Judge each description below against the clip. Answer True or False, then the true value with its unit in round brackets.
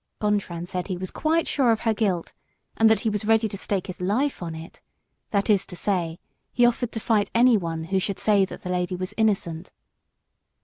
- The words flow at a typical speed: False (210 wpm)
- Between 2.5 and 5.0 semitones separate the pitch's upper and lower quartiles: True (3.7 semitones)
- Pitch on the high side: True (200 Hz)